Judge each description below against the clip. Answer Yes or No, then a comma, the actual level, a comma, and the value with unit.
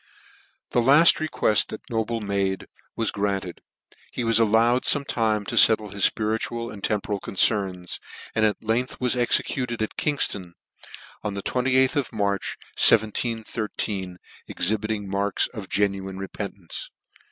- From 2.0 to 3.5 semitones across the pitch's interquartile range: Yes, average, 2.8 semitones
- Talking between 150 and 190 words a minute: No, slow, 135 wpm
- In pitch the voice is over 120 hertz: No, low, 110 Hz